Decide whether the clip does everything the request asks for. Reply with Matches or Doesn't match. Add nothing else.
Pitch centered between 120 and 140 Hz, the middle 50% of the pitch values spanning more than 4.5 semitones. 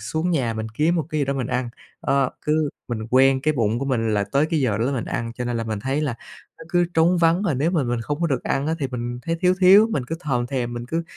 Matches